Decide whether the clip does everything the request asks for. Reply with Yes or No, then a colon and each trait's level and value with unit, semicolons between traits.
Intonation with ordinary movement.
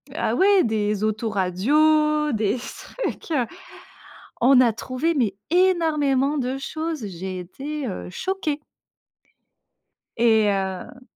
No: wide, 6.3 semitones